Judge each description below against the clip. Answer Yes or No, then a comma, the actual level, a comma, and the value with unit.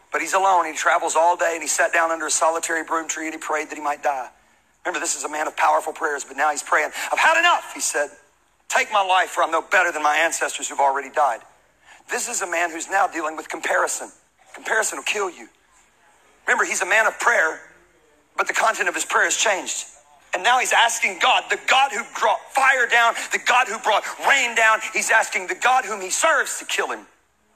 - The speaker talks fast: Yes, fast, 235 wpm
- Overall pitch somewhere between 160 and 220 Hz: Yes, medium, 185 Hz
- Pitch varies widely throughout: Yes, wide, 6.5 semitones